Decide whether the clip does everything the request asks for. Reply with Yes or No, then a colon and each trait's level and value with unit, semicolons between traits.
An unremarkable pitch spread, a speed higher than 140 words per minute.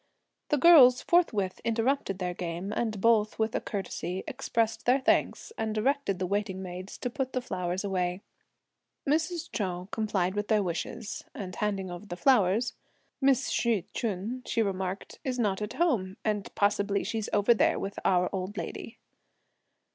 Yes: average, 4.0 semitones; average, 160 wpm